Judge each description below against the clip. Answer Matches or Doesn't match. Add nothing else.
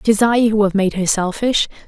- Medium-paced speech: Doesn't match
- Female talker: Matches